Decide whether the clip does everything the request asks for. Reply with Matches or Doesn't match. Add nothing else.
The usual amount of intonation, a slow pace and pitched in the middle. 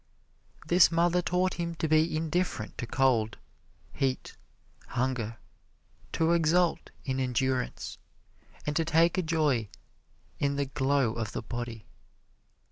Matches